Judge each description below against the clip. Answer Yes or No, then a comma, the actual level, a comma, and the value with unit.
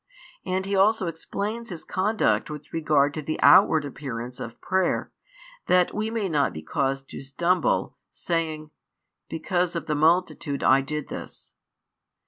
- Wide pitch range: No, average, 4.4 semitones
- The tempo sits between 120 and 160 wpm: Yes, average, 145 wpm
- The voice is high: No, medium, 160 Hz